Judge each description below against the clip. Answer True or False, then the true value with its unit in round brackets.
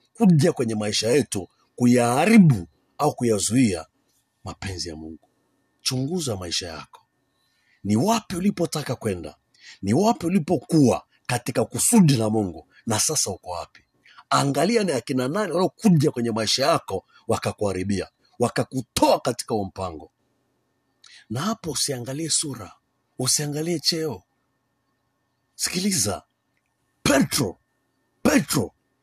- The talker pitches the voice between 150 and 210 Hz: False (135 Hz)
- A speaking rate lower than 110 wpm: True (100 wpm)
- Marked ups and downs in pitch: True (7.2 semitones)